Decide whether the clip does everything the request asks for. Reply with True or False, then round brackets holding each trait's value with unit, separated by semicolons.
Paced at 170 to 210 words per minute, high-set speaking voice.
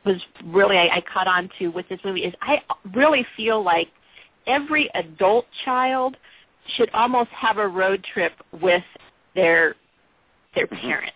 False (150 wpm; 210 Hz)